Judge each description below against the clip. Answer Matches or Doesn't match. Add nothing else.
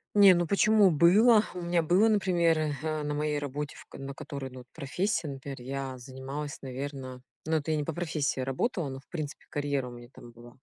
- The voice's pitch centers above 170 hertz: Doesn't match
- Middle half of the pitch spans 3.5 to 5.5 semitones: Matches